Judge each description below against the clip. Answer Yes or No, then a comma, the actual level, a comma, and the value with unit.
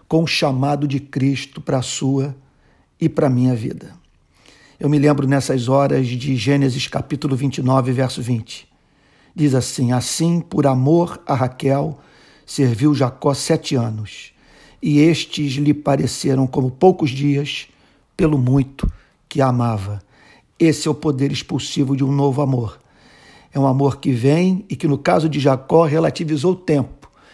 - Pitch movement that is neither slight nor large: No, narrow, 2.2 semitones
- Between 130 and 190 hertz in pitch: Yes, medium, 140 Hz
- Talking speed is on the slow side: No, average, 155 wpm